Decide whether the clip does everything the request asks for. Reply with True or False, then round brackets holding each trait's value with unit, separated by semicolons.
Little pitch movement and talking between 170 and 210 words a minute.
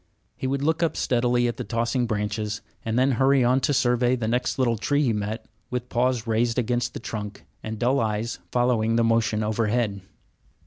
True (2.2 semitones; 190 wpm)